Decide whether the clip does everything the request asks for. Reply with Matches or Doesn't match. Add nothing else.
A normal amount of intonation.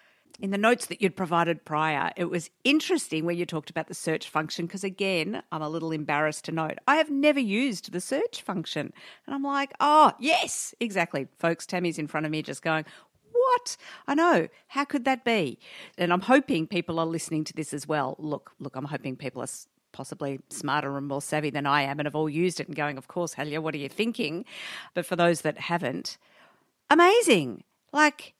Doesn't match